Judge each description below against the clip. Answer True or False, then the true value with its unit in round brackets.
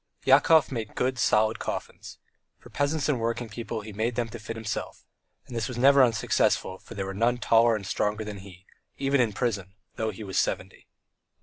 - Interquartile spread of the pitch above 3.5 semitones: False (2.8 semitones)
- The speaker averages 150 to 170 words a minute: False (200 wpm)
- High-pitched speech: False (115 Hz)